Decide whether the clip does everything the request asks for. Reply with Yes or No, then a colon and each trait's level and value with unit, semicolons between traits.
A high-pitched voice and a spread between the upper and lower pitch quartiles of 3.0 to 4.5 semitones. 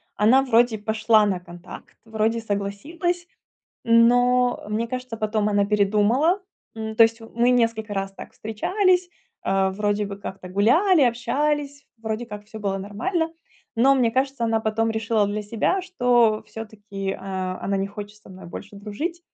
Yes: high, 220 Hz; average, 3.3 semitones